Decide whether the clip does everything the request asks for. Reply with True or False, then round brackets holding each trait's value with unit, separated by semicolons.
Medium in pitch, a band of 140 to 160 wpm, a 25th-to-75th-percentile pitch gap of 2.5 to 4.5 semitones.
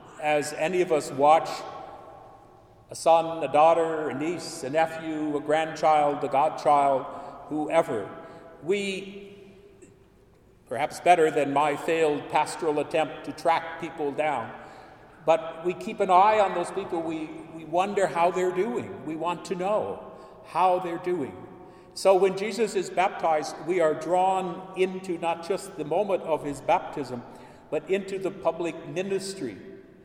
True (165 Hz; 145 wpm; 3.2 semitones)